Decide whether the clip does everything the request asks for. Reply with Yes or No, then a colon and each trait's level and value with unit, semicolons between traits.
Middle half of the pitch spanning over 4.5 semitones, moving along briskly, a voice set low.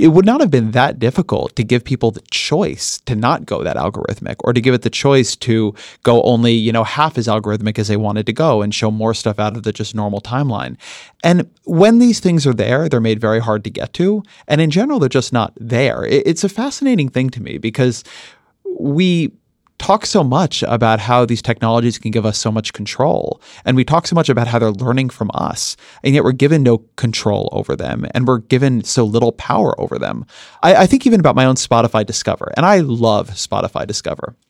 Yes: average, 5.1 semitones; fast, 225 wpm; low, 120 Hz